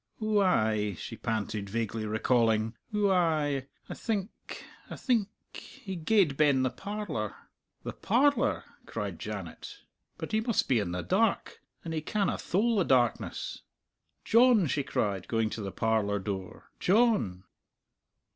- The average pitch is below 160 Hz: Yes, medium, 140 Hz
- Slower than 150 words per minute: Yes, average, 140 wpm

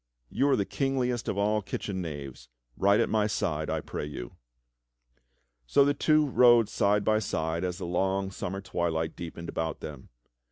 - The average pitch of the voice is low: Yes, very low, 95 Hz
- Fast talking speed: No, average, 170 wpm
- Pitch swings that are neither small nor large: Yes, average, 5.0 semitones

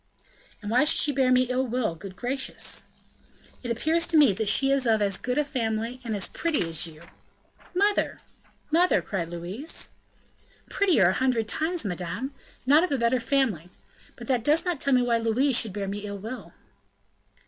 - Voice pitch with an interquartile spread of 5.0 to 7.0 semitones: Yes, average, 5.3 semitones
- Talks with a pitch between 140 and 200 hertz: No, high, 245 Hz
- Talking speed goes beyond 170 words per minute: Yes, average, 185 wpm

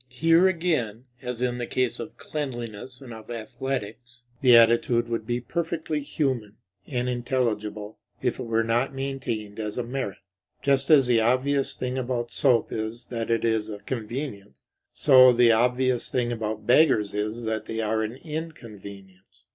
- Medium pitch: No, low, 120 Hz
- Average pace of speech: Yes, average, 160 wpm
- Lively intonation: No, average, 3.0 semitones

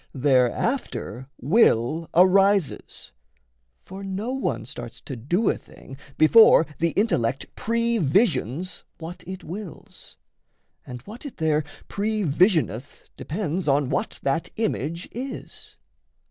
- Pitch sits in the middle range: Yes, medium, 175 Hz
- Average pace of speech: No, slow, 110 wpm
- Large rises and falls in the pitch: Yes, wide, 6.9 semitones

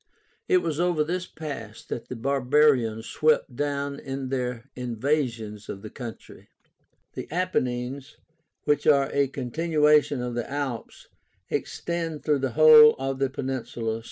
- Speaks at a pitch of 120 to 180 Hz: Yes, low, 135 Hz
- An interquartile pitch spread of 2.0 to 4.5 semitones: Yes, average, 3.6 semitones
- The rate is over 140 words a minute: No, slow, 135 wpm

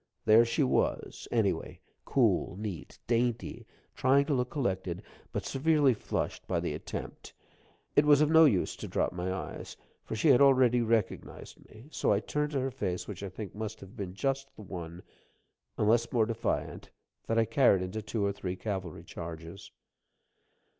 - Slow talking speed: No, average, 175 wpm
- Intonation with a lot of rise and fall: Yes, wide, 5.8 semitones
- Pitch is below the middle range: Yes, low, 110 Hz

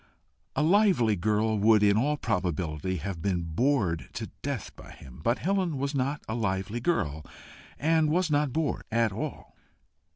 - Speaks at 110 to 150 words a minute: No, average, 160 wpm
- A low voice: Yes, low, 115 Hz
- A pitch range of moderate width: No, wide, 7.7 semitones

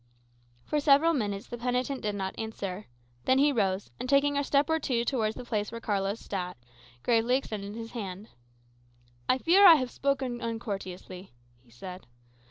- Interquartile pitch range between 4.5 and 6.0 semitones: Yes, average, 5.3 semitones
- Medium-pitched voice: No, high, 230 Hz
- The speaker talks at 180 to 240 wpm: No, average, 170 wpm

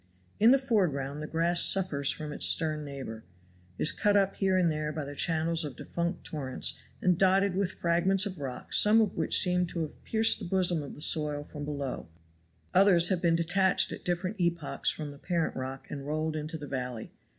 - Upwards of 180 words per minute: Yes, average, 200 wpm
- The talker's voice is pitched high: No, medium, 165 Hz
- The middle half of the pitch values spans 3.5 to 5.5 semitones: Yes, average, 4.0 semitones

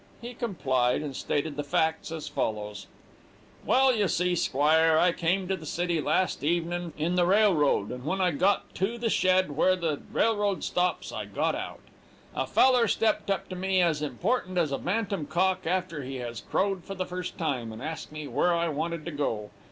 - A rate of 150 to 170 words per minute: No, average, 200 wpm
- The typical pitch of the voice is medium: Yes, medium, 170 Hz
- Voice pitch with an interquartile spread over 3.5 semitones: Yes, average, 4.2 semitones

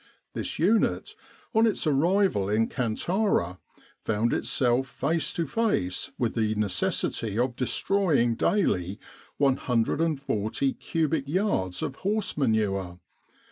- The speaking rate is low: Yes, slow, 105 wpm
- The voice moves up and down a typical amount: No, wide, 7.4 semitones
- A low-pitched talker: Yes, low, 130 Hz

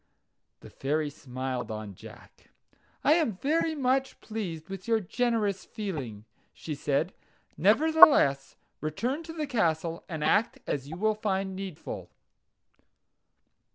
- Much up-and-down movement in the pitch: Yes, wide, 8.1 semitones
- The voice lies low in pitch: No, high, 190 Hz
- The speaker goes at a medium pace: No, slow, 120 wpm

